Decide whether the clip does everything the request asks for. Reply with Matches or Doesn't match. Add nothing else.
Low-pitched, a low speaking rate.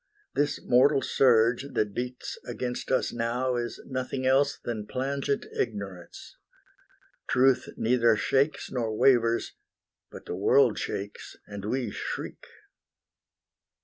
Matches